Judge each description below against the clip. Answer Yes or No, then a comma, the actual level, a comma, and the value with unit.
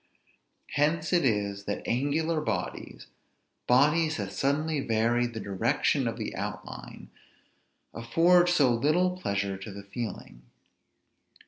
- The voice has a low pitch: Yes, low, 125 Hz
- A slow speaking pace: Yes, slow, 115 wpm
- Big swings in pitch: Yes, wide, 7.5 semitones